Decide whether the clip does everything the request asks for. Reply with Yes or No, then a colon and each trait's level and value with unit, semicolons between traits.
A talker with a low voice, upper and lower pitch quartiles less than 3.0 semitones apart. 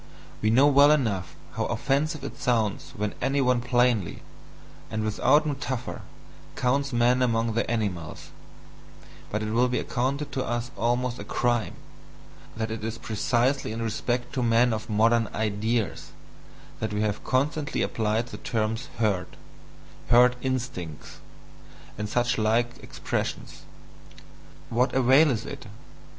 Yes: low, 120 Hz; narrow, 2.6 semitones